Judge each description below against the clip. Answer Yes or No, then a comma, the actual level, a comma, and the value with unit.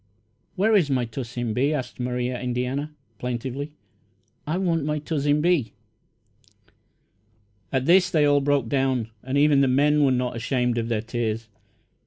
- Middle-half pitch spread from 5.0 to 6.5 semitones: No, average, 3.2 semitones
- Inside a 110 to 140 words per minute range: No, average, 150 wpm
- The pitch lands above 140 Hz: No, low, 135 Hz